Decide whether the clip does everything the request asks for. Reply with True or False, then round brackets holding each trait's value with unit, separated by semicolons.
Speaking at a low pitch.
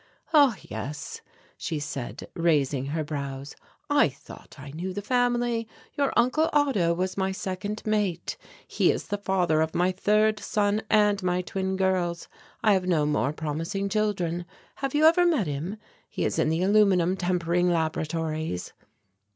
False (185 Hz)